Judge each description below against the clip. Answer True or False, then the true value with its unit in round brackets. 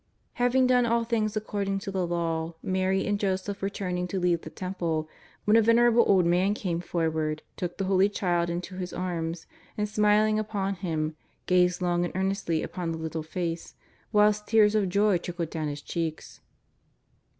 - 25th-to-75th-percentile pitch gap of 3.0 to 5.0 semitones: True (3.4 semitones)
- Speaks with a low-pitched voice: False (185 Hz)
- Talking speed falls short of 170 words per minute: False (175 wpm)